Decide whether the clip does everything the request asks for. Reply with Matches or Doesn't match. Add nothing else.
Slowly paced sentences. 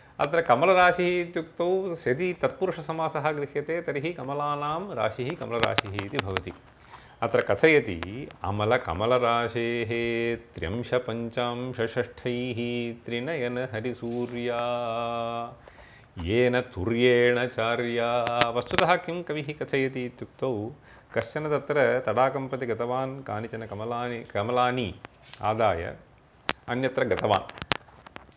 Matches